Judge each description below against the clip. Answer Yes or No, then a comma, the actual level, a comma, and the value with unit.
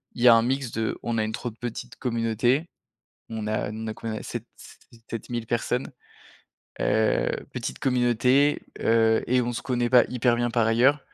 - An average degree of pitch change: No, narrow, 1.8 semitones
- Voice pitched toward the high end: No, low, 120 Hz